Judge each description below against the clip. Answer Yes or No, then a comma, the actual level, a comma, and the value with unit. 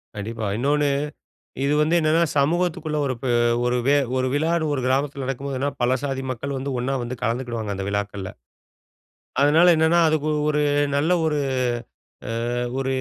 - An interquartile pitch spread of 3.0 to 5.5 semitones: Yes, average, 3.5 semitones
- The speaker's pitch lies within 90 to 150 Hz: Yes, medium, 140 Hz